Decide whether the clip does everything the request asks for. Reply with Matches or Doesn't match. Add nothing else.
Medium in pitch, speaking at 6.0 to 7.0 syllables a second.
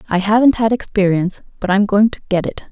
Doesn't match